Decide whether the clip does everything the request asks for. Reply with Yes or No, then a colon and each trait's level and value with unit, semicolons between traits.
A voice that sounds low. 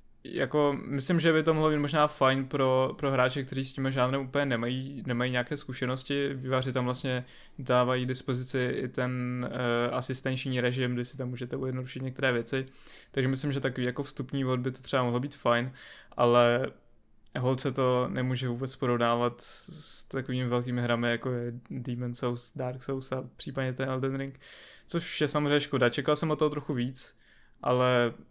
Yes: low, 130 Hz